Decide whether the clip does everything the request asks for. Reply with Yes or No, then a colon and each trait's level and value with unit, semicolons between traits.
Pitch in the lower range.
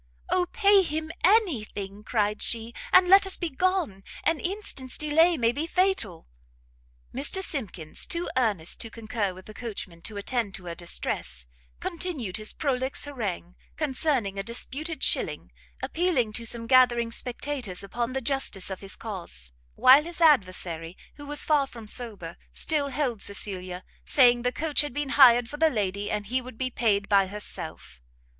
No: high, 240 Hz